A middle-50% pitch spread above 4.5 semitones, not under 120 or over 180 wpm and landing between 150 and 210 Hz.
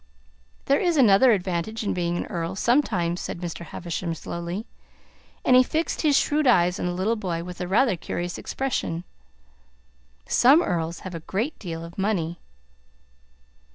Yes: wide, 5.6 semitones; average, 155 wpm; medium, 185 Hz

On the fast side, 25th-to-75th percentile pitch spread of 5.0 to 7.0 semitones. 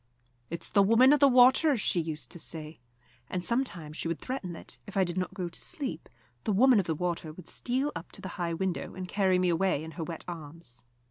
Yes: fast, 230 wpm; average, 5.3 semitones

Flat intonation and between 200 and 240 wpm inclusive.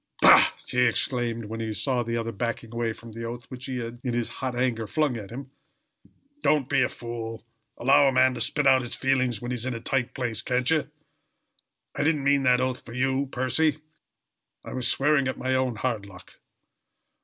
Yes: narrow, 2.3 semitones; fast, 205 wpm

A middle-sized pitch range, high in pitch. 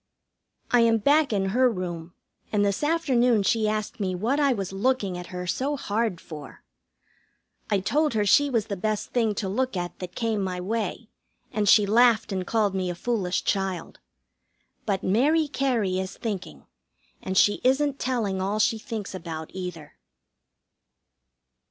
Yes: average, 4.4 semitones; high, 210 Hz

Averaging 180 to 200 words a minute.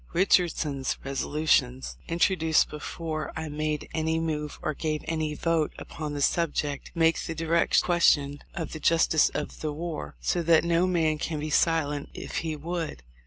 No: average, 165 wpm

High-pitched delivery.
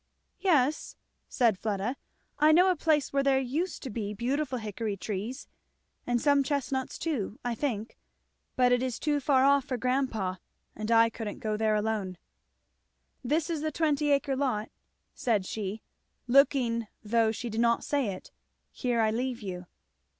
Yes: high, 245 Hz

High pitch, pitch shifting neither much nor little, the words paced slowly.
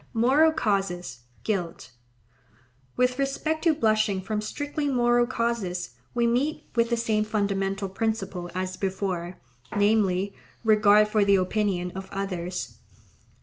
Yes: high, 205 Hz; average, 4.1 semitones; slow, 115 wpm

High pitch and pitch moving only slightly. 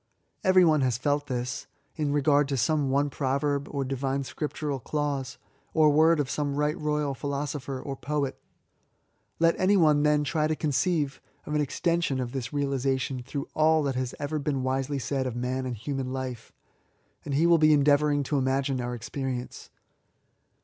No: medium, 140 Hz; narrow, 2.2 semitones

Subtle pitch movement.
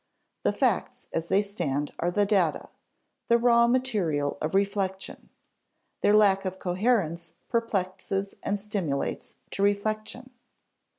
No: average, 3.3 semitones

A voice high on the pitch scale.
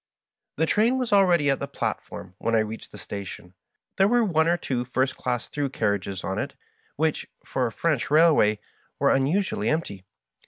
No: medium, 140 Hz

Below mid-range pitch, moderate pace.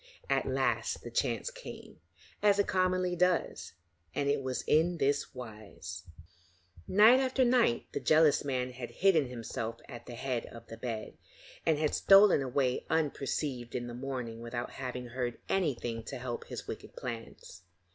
Yes: low, 130 Hz; average, 155 wpm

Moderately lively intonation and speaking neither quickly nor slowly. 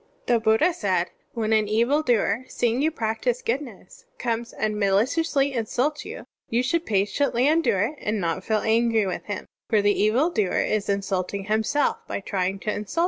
Yes: average, 3.7 semitones; average, 190 wpm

